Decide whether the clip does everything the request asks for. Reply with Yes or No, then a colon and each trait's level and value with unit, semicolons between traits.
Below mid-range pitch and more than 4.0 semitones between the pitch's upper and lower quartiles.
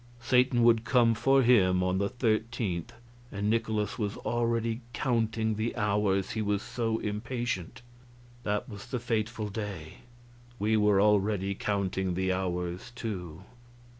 No: low, 105 Hz; average, 3.0 semitones